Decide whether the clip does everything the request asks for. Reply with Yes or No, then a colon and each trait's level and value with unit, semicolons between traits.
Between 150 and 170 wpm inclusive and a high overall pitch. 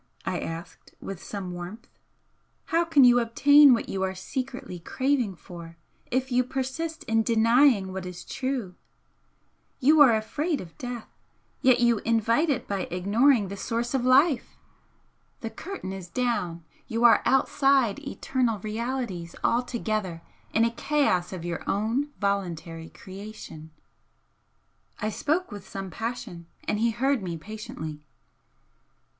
No: slow, 135 wpm; high, 225 Hz